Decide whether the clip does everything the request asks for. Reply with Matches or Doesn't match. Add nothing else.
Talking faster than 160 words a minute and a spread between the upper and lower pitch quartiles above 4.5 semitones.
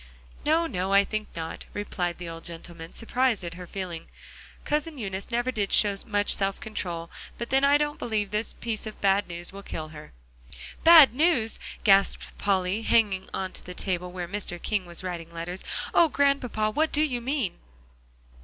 Matches